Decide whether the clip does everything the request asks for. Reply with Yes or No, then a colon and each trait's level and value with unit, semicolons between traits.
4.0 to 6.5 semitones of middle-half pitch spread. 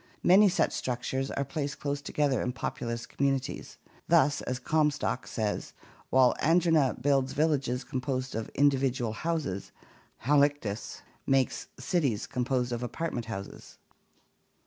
No: average, 2.9 semitones